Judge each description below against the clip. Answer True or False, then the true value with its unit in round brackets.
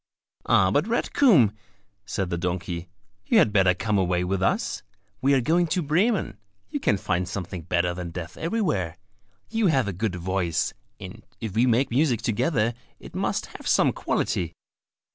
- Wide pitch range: True (7.2 semitones)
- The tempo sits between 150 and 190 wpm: True (170 wpm)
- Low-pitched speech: True (100 Hz)